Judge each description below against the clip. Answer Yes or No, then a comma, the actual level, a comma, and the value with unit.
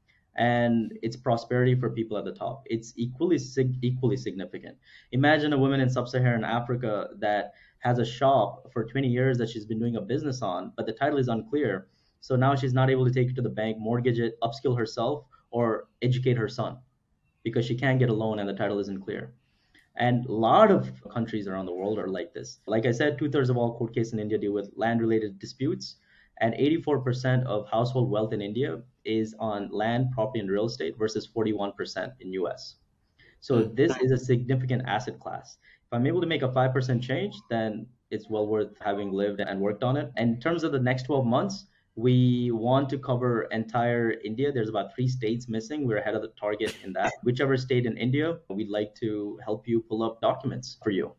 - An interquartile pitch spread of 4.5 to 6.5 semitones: No, average, 2.8 semitones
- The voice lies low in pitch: Yes, low, 120 Hz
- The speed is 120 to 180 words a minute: No, fast, 205 wpm